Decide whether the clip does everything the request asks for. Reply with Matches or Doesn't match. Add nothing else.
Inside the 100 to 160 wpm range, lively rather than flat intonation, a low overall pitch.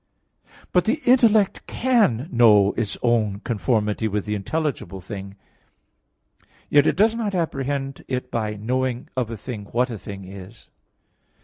Matches